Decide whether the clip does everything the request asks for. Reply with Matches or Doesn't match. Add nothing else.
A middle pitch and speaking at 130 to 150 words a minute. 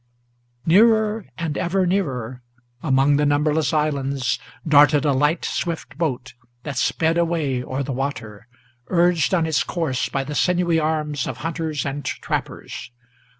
Matches